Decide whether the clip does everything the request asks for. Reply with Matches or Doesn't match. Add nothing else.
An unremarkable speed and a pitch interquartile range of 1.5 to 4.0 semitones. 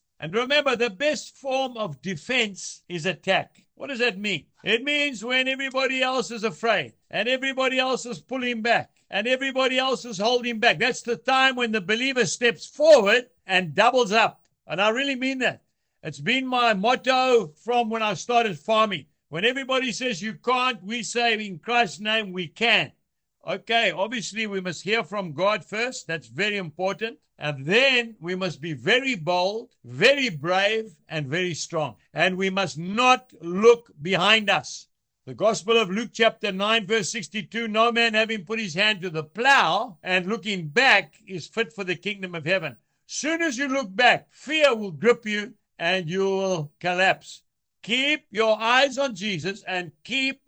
Doesn't match